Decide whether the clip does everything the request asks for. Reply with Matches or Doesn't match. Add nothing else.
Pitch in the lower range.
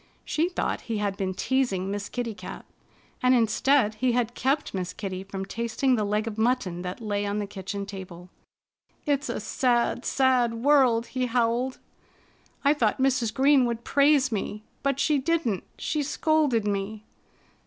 Doesn't match